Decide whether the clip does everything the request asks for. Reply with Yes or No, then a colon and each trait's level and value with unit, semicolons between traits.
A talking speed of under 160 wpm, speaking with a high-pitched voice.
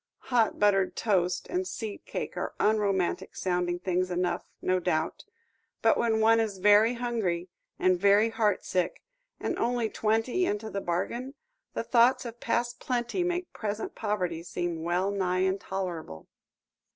Yes: average, 140 wpm; high, 205 Hz